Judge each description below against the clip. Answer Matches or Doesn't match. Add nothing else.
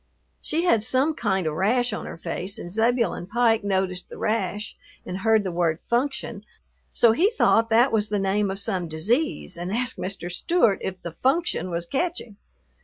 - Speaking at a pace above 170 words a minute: Matches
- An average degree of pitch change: Matches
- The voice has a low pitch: Doesn't match